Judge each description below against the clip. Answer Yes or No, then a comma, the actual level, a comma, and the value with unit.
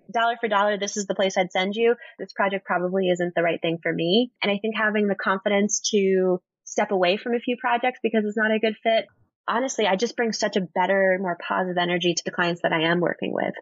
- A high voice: Yes, high, 200 Hz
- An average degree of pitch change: Yes, average, 3.5 semitones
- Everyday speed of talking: No, fast, 245 wpm